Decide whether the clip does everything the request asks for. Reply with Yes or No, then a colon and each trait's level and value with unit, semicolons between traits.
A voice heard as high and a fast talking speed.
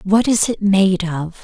Yes: high, 195 Hz; fast, 210 wpm